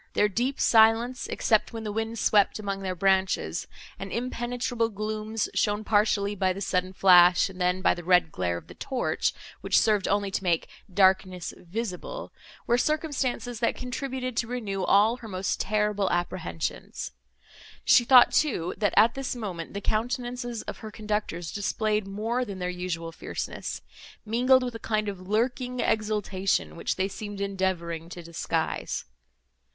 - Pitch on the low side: No, high, 210 Hz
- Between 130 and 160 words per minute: Yes, average, 155 wpm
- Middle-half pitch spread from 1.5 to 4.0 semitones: Yes, average, 3.7 semitones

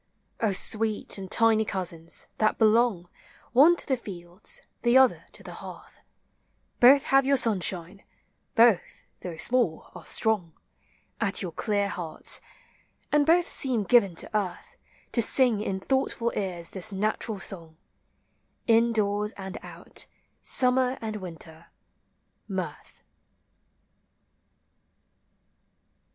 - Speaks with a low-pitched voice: No, high, 210 Hz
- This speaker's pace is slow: Yes, slow, 120 wpm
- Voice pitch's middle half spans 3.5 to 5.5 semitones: Yes, average, 4.4 semitones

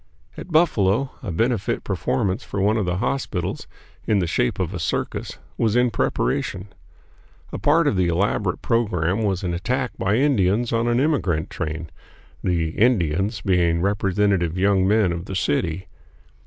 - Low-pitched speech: Yes, low, 100 Hz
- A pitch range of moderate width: Yes, average, 4.4 semitones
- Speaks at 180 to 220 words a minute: No, average, 155 wpm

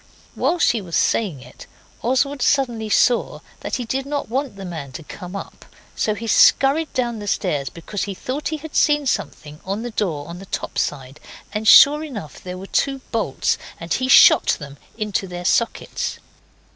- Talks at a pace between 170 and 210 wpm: Yes, average, 185 wpm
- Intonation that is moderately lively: No, wide, 6.9 semitones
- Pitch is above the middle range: Yes, high, 215 Hz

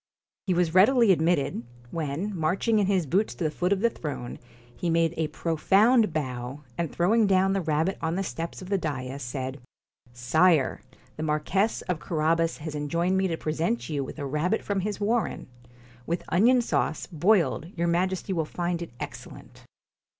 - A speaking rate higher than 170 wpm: Yes, average, 180 wpm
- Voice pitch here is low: No, medium, 170 Hz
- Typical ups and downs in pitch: Yes, average, 4.0 semitones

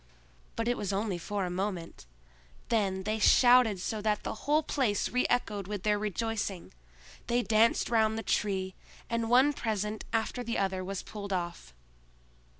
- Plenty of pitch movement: No, average, 2.9 semitones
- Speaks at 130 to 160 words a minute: Yes, average, 155 wpm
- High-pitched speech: Yes, high, 210 Hz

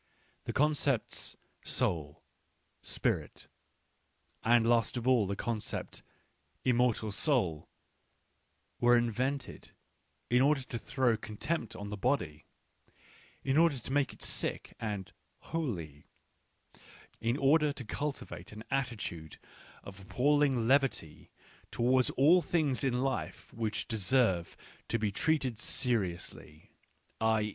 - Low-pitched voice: Yes, low, 120 Hz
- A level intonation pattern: No, average, 4.4 semitones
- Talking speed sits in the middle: No, slow, 120 wpm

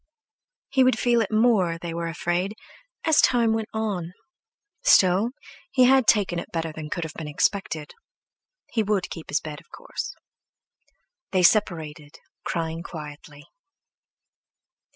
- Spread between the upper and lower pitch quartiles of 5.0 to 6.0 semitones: Yes, average, 5.3 semitones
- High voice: No, medium, 180 Hz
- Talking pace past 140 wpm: No, slow, 135 wpm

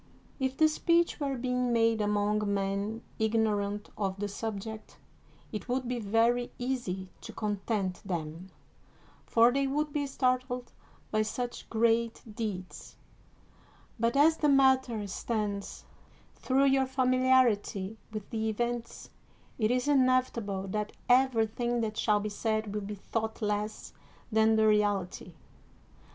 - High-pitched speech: Yes, high, 225 Hz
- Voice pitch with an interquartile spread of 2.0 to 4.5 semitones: Yes, average, 3.5 semitones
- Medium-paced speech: No, slow, 130 wpm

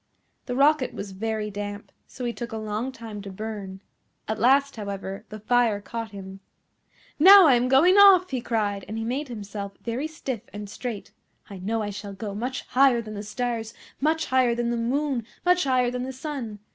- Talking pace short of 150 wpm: No, average, 195 wpm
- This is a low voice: No, high, 230 Hz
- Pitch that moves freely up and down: No, average, 3.9 semitones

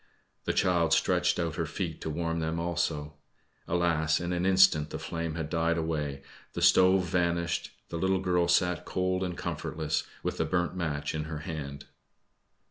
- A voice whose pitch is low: Yes, very low, 85 Hz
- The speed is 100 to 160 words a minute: No, average, 170 wpm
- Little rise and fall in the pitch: Yes, narrow, 2.2 semitones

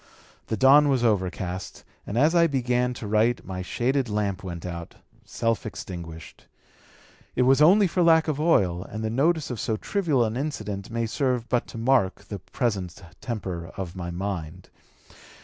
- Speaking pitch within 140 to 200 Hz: No, low, 115 Hz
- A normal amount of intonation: No, wide, 6.1 semitones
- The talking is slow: No, average, 165 wpm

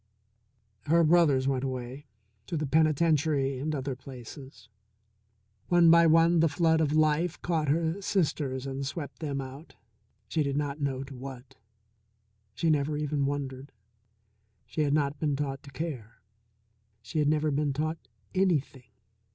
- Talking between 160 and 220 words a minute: No, average, 145 wpm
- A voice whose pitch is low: No, medium, 145 Hz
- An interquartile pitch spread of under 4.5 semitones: Yes, average, 2.8 semitones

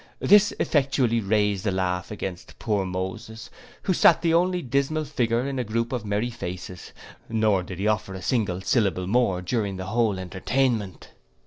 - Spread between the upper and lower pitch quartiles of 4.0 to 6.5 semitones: Yes, average, 4.8 semitones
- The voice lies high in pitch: No, low, 110 Hz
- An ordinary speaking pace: Yes, average, 170 wpm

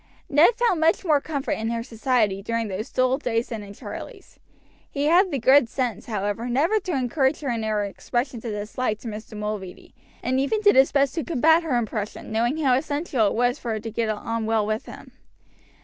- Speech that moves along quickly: Yes, fast, 210 wpm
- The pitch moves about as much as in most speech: Yes, average, 4.5 semitones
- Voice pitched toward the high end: Yes, high, 245 Hz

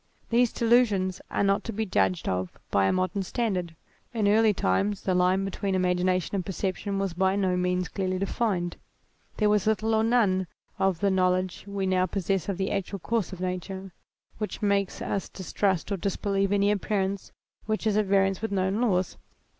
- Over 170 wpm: Yes, average, 185 wpm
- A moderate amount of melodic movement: No, narrow, 1.9 semitones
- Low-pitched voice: No, high, 195 Hz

